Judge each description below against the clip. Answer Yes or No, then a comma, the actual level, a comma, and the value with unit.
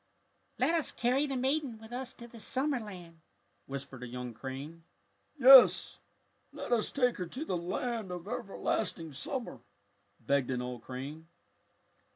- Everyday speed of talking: Yes, average, 155 wpm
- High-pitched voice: Yes, high, 195 Hz